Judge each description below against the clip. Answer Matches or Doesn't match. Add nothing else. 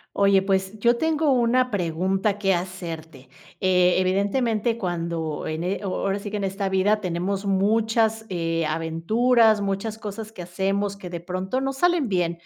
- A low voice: Doesn't match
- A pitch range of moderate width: Matches